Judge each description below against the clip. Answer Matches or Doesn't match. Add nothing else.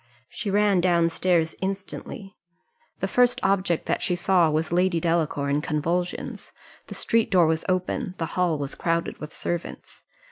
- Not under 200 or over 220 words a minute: Doesn't match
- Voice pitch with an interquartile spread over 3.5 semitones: Doesn't match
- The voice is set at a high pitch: Doesn't match